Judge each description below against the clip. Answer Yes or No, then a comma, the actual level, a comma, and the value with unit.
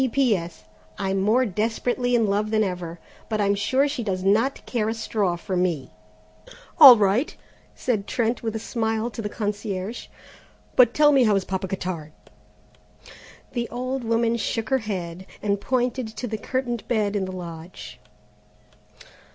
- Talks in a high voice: Yes, high, 215 Hz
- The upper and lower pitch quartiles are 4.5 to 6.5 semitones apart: No, average, 4.0 semitones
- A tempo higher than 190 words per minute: No, average, 160 wpm